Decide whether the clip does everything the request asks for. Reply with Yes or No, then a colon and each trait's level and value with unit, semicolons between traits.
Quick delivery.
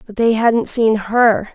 No: average, 195 wpm